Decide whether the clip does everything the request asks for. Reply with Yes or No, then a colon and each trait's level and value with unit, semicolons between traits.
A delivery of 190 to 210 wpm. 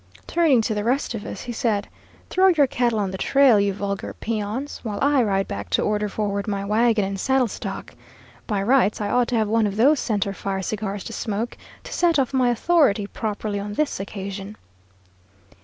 Yes: average, 200 wpm